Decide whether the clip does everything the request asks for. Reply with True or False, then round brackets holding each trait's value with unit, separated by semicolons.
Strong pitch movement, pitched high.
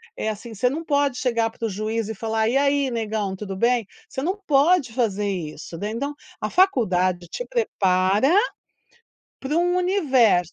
True (5.8 semitones; 230 Hz)